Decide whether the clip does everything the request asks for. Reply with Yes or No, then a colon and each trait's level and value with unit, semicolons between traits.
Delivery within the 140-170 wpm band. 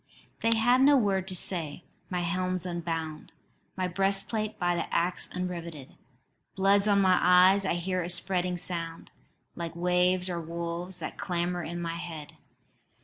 Yes: average, 150 wpm